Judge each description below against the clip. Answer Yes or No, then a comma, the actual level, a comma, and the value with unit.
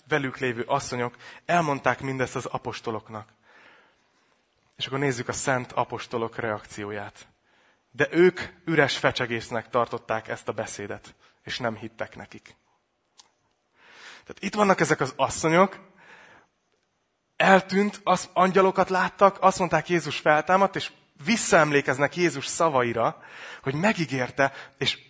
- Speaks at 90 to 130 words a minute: Yes, average, 110 wpm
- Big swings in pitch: Yes, wide, 6.2 semitones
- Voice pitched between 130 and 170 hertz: Yes, medium, 140 Hz